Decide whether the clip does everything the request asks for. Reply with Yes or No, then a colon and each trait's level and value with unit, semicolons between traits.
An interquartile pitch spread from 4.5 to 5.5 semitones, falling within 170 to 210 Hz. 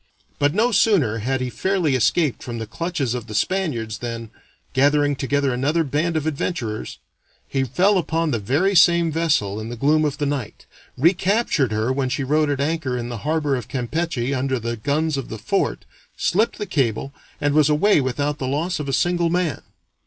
No: average, 4.8 semitones; medium, 145 Hz